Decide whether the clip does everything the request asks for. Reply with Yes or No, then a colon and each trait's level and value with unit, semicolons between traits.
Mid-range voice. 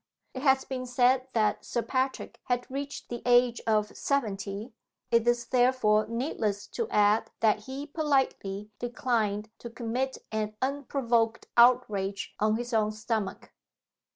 No: high, 235 Hz